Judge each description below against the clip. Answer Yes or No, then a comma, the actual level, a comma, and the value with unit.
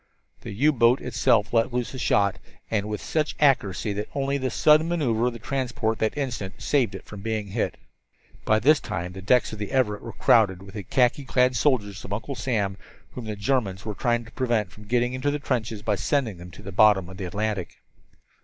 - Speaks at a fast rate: Yes, fast, 220 wpm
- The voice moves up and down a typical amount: Yes, average, 4.0 semitones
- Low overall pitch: Yes, low, 110 Hz